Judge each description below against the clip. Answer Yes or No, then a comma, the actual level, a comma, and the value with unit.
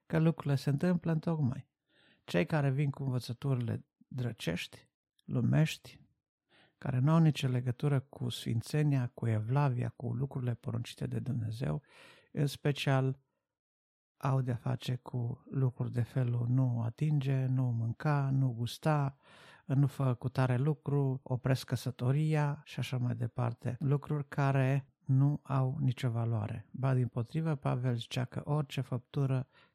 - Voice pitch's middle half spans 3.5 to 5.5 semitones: No, narrow, 2.6 semitones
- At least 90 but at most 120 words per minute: No, average, 135 wpm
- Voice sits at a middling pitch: No, low, 130 Hz